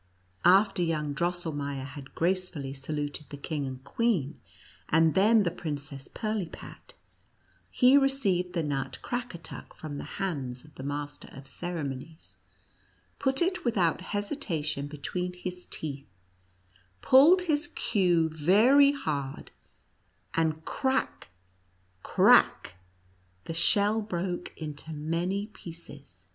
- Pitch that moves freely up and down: Yes, wide, 5.8 semitones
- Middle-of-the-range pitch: Yes, medium, 165 Hz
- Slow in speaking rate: Yes, slow, 120 wpm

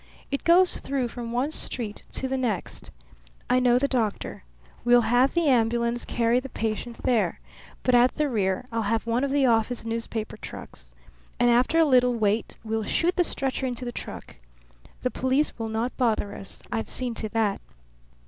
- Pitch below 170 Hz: No, high, 240 Hz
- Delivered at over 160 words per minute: Yes, average, 180 wpm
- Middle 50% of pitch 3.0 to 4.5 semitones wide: No, narrow, 2.4 semitones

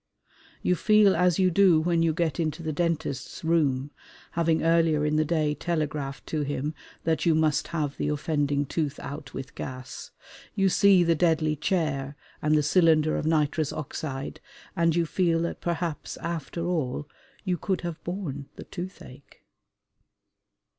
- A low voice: No, medium, 160 Hz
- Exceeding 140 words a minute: Yes, average, 155 wpm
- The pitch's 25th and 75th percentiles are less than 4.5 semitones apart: Yes, narrow, 2.6 semitones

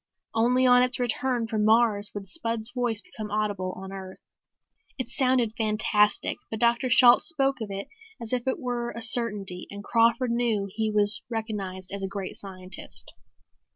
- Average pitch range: Yes, average, 3.1 semitones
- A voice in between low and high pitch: No, high, 220 Hz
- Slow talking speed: No, average, 165 wpm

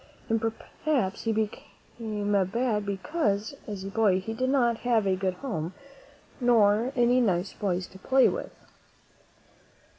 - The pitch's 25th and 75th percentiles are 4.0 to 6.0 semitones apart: No, average, 3.5 semitones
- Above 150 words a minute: No, average, 145 wpm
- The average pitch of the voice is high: Yes, high, 215 Hz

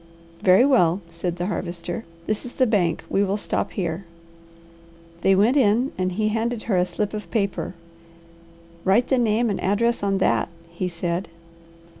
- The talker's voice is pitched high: Yes, high, 200 Hz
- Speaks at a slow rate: No, average, 165 wpm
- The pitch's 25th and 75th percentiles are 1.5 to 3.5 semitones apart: No, average, 3.9 semitones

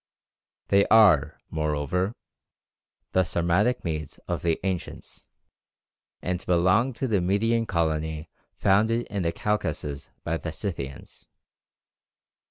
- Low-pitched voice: Yes, very low, 90 Hz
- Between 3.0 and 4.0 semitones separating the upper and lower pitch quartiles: No, average, 4.8 semitones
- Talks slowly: Yes, slow, 105 wpm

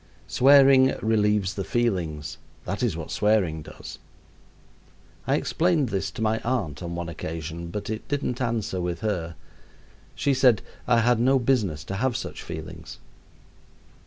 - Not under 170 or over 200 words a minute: No, average, 145 wpm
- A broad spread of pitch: Yes, wide, 6.3 semitones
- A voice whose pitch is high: No, low, 105 Hz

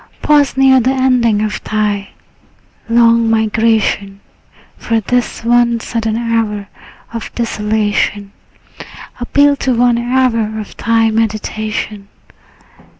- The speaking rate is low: Yes, slow, 100 wpm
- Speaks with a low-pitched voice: No, high, 225 Hz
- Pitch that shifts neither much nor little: No, narrow, 2.1 semitones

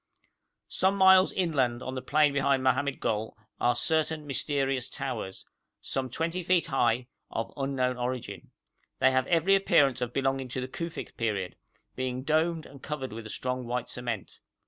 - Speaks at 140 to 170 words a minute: Yes, average, 160 wpm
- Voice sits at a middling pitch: No, low, 130 Hz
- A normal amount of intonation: Yes, average, 3.6 semitones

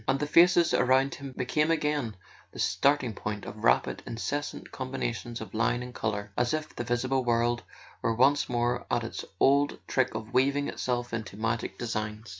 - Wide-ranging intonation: No, average, 3.5 semitones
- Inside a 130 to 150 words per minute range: No, average, 180 wpm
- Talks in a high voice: No, low, 120 Hz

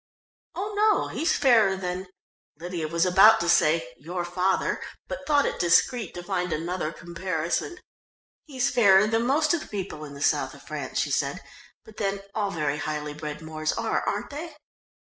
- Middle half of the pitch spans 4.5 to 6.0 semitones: Yes, wide, 5.6 semitones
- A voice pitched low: No, medium, 185 Hz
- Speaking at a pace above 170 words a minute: Yes, average, 180 wpm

